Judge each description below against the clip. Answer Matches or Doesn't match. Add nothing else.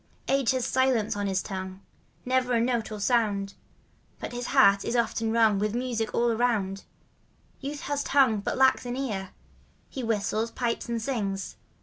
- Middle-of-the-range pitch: Doesn't match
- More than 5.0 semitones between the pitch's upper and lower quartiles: Doesn't match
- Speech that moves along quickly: Doesn't match